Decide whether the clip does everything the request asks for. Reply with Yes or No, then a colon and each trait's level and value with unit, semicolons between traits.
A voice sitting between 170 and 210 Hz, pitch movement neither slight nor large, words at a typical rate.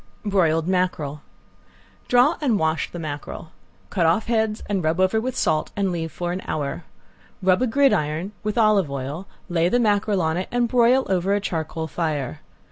Yes: medium, 185 Hz; average, 4.9 semitones; average, 175 wpm